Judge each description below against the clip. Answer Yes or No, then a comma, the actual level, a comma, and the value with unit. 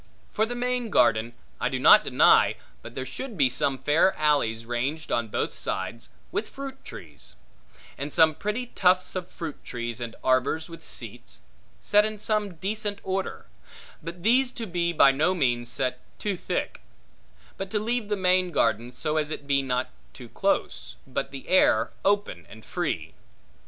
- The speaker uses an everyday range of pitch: No, wide, 8.3 semitones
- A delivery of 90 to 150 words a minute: No, average, 165 wpm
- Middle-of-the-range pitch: Yes, medium, 160 Hz